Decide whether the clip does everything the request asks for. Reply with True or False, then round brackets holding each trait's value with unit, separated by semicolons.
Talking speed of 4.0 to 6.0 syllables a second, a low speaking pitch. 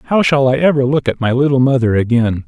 False (6.2 syllables/s; 130 Hz)